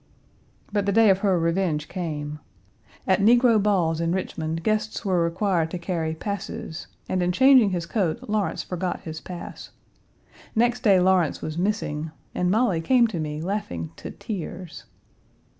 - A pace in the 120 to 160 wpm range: Yes, average, 155 wpm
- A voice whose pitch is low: No, medium, 185 Hz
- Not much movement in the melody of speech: No, average, 4.2 semitones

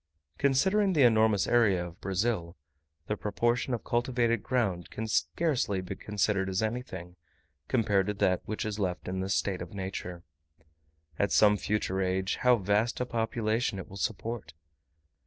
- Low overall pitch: Yes, low, 105 Hz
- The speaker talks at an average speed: Yes, average, 155 wpm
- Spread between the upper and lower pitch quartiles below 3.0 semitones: No, average, 4.0 semitones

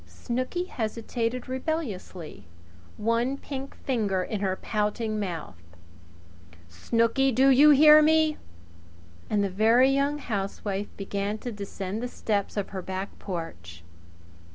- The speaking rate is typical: No, slow, 120 wpm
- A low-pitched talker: No, high, 220 Hz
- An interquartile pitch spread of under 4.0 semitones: No, average, 5.2 semitones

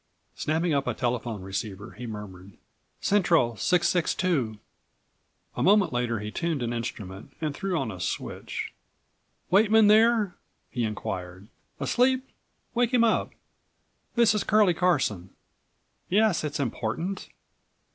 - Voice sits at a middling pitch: Yes, medium, 150 Hz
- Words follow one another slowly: Yes, slow, 120 wpm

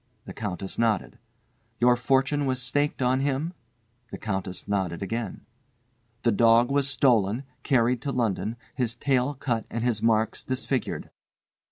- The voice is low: Yes, low, 120 Hz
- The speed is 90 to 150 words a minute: Yes, average, 140 wpm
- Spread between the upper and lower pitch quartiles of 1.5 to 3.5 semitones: Yes, average, 3.2 semitones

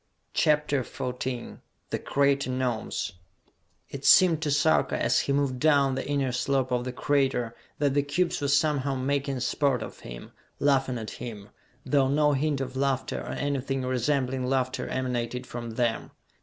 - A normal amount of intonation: No, narrow, 2.1 semitones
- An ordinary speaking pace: Yes, average, 155 wpm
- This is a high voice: No, low, 135 Hz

